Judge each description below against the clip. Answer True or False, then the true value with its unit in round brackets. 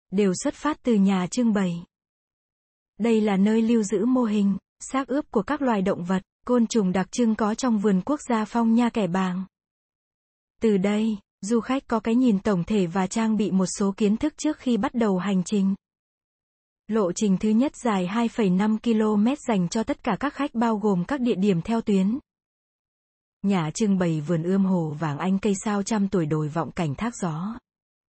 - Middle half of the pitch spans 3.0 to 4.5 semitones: True (3.4 semitones)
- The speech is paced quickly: False (200 wpm)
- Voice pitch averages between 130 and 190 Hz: False (215 Hz)